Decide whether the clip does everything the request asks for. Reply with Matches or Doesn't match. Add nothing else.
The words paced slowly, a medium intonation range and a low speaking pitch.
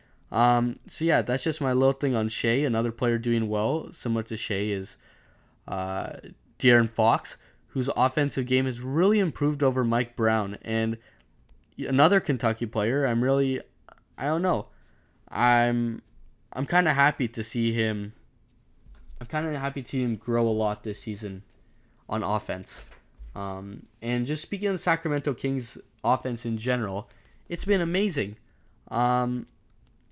Doesn't match